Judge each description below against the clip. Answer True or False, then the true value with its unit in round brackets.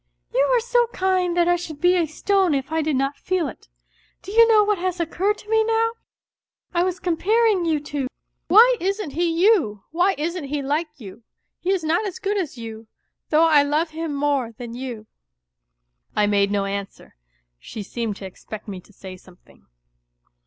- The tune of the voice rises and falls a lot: True (6.9 semitones)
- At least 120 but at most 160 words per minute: True (155 wpm)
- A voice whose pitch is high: True (320 Hz)